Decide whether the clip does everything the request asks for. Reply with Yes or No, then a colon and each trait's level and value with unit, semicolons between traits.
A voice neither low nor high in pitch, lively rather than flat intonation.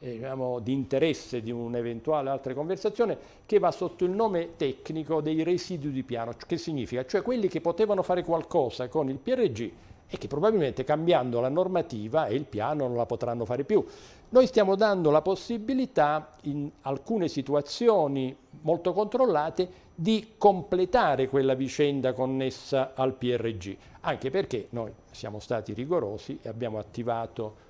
Yes: medium, 150 Hz; wide, 6.3 semitones